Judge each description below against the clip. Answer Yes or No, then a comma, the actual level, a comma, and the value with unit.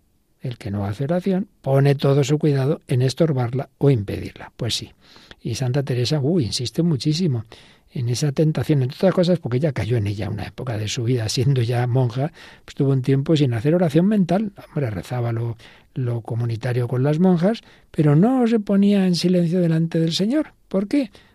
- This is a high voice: No, medium, 140 Hz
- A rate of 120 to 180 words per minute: No, fast, 190 wpm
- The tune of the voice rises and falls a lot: Yes, wide, 5.8 semitones